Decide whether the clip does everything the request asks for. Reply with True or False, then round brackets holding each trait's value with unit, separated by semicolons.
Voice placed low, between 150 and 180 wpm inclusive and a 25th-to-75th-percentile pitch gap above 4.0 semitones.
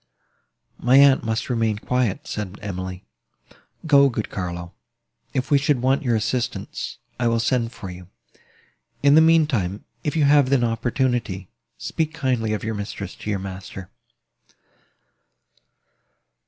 False (115 Hz; 140 wpm; 5.2 semitones)